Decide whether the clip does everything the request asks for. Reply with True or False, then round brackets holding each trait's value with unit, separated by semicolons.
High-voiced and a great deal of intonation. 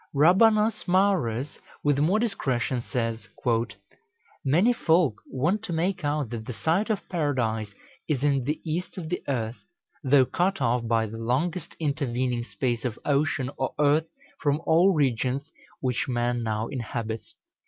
False (140 Hz; 5.7 semitones)